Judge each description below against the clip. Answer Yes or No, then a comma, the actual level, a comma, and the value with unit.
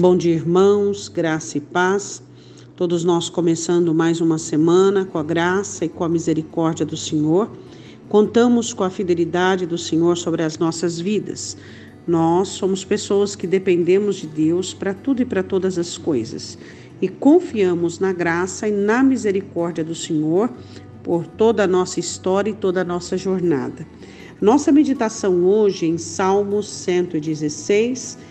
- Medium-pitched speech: Yes, medium, 180 Hz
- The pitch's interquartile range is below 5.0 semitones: Yes, average, 3.0 semitones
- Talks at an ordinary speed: Yes, average, 150 wpm